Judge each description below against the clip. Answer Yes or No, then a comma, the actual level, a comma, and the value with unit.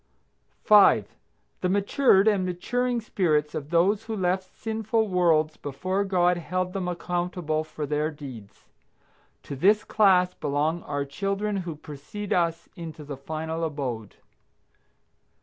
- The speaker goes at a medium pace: No, slow, 130 wpm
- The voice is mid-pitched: Yes, medium, 175 Hz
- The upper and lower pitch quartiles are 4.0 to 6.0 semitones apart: Yes, average, 4.4 semitones